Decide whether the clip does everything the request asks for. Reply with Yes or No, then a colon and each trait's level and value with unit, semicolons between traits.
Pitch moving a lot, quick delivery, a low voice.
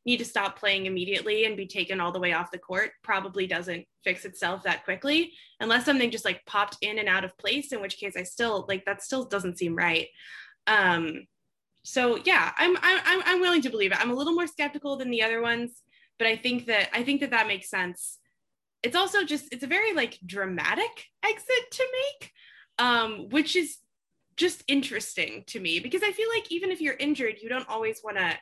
No: wide, 7.8 semitones; fast, 215 wpm; high, 235 Hz